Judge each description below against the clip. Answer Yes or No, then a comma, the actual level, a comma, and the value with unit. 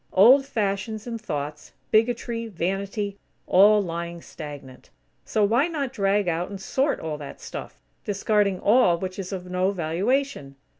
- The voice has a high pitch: Yes, high, 200 Hz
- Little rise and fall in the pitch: No, average, 4.5 semitones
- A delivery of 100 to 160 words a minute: Yes, average, 145 wpm